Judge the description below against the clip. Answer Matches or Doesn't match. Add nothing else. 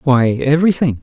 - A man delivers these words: Matches